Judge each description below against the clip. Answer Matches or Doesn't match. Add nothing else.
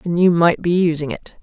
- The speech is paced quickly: Matches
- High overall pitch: Doesn't match